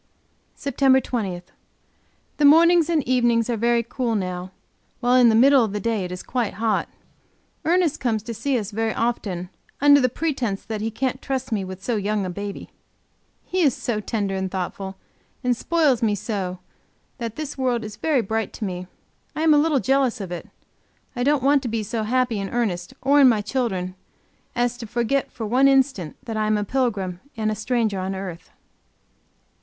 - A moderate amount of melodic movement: Yes, average, 4.4 semitones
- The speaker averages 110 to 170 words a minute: No, average, 190 wpm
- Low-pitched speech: No, high, 230 Hz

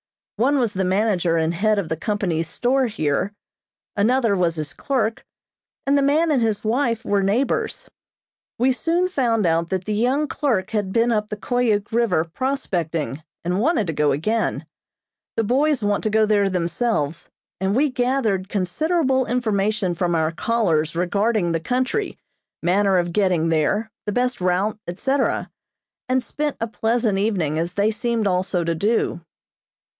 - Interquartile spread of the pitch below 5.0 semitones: No, wide, 5.5 semitones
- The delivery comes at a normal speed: Yes, average, 160 wpm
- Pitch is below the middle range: No, high, 210 Hz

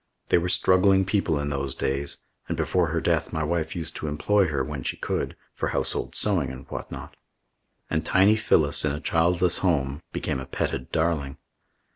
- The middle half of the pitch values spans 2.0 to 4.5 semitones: Yes, average, 4.0 semitones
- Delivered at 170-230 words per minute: Yes, average, 180 wpm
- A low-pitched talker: Yes, very low, 80 Hz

